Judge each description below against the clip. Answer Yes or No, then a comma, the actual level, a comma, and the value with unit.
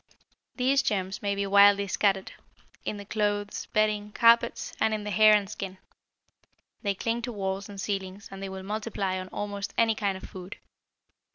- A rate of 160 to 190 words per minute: Yes, average, 175 wpm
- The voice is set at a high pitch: Yes, high, 205 Hz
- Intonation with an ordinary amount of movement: No, narrow, 1.7 semitones